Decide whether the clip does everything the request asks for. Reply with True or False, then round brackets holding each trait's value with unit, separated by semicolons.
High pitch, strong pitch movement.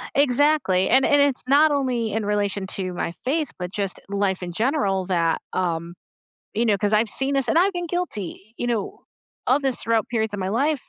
True (220 Hz; 6.3 semitones)